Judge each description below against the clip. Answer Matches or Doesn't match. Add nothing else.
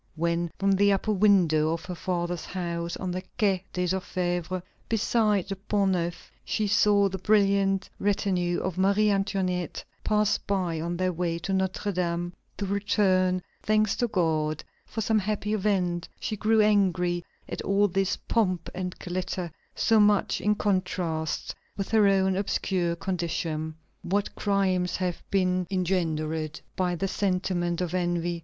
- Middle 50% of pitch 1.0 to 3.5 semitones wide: Matches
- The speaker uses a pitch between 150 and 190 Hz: Matches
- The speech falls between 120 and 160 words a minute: Matches